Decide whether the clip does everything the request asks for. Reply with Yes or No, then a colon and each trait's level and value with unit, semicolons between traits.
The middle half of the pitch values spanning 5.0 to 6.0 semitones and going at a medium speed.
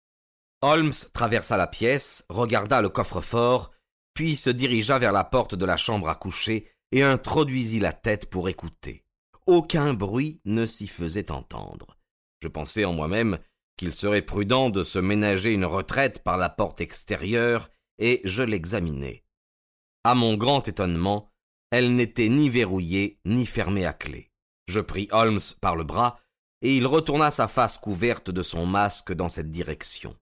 Yes: wide, 5.4 semitones; average, 155 wpm